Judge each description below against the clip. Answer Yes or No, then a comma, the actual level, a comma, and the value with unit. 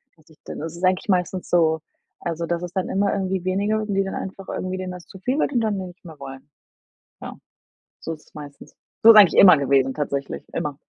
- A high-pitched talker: No, medium, 180 Hz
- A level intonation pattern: No, average, 3.5 semitones